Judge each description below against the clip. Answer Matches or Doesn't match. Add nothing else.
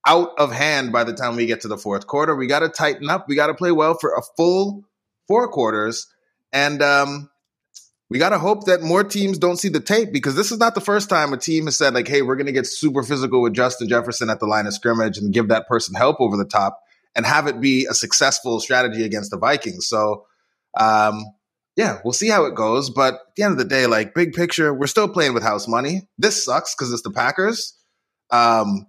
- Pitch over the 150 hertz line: Doesn't match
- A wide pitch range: Matches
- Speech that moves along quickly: Matches